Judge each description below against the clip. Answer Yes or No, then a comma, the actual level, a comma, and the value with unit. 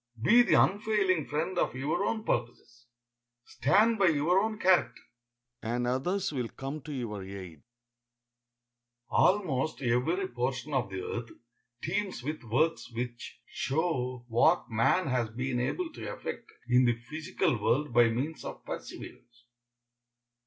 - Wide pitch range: Yes, wide, 6.6 semitones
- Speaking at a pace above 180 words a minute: No, slow, 135 wpm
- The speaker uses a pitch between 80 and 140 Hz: Yes, low, 135 Hz